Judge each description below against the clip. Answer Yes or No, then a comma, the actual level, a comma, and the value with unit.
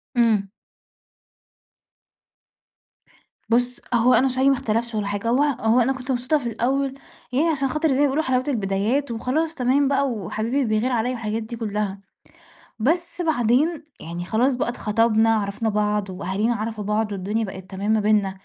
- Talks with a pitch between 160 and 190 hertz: No, high, 235 Hz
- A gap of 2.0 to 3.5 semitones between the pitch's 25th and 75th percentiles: No, average, 4.1 semitones